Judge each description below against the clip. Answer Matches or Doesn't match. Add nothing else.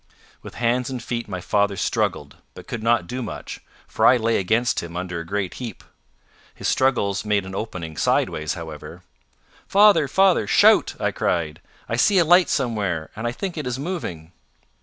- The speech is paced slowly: Doesn't match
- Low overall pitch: Matches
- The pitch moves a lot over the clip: Matches